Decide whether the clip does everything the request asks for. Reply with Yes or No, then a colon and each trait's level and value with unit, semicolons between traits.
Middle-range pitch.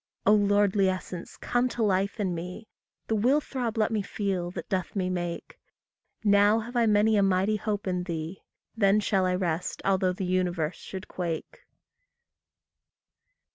No: high, 195 Hz